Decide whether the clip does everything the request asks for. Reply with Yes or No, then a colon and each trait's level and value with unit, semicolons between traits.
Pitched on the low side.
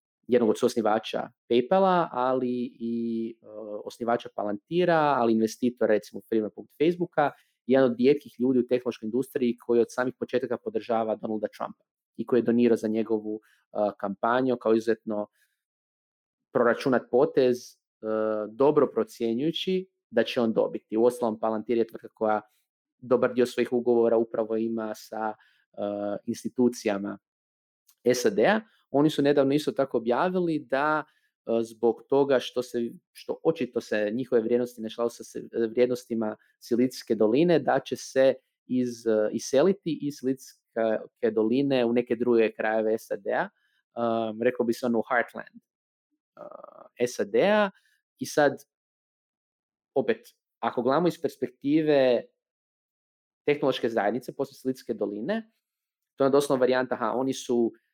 Yes: low, 120 Hz